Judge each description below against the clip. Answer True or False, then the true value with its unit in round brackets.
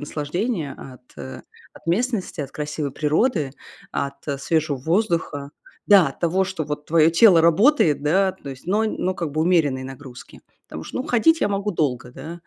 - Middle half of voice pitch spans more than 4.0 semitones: True (5.0 semitones)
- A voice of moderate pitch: True (160 Hz)